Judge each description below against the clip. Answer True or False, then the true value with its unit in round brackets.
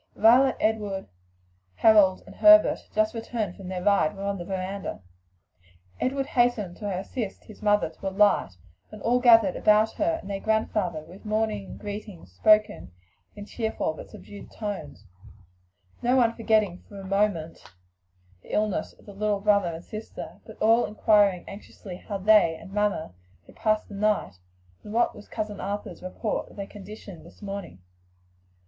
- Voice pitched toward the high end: True (205 Hz)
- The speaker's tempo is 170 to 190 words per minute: False (160 wpm)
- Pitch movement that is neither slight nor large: False (2.2 semitones)